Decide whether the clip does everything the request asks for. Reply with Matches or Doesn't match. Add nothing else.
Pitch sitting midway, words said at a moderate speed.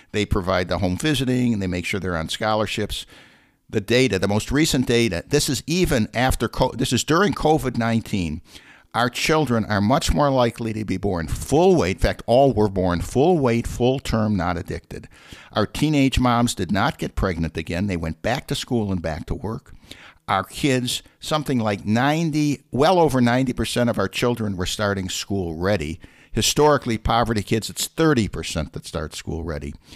Doesn't match